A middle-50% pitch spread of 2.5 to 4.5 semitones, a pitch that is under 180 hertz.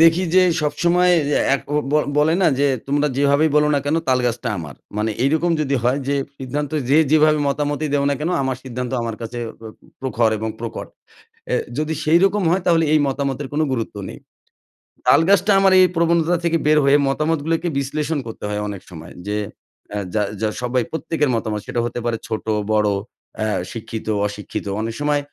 No: average, 5.3 semitones; medium, 140 Hz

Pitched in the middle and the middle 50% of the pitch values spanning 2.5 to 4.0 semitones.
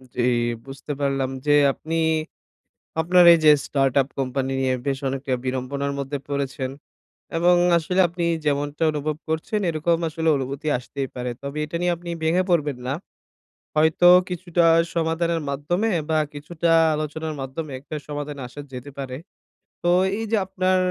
Yes: medium, 150 Hz; average, 3.5 semitones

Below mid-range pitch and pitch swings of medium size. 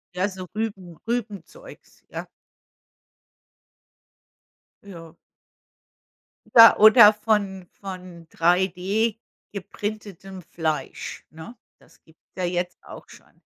No: high, 190 Hz; average, 3.2 semitones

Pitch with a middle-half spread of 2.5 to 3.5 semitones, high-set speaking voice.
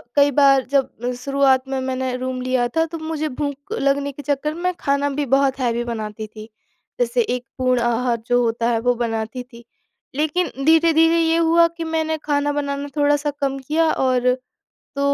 Yes: average, 3.2 semitones; very high, 275 Hz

